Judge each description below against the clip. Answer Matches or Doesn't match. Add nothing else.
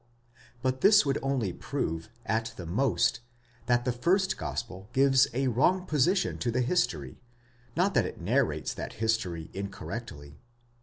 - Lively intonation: Matches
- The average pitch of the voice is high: Doesn't match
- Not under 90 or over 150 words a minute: Matches